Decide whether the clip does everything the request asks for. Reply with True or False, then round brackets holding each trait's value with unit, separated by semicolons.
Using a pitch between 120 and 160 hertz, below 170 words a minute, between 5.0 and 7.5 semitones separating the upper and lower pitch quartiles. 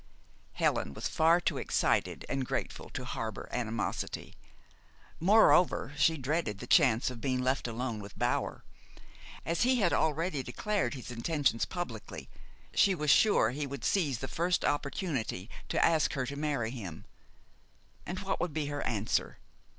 True (140 Hz; 150 wpm; 5.5 semitones)